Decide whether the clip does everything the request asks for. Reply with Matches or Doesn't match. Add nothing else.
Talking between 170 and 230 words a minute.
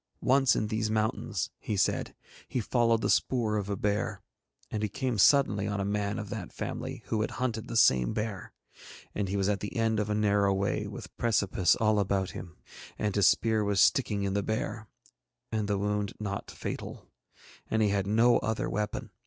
Matches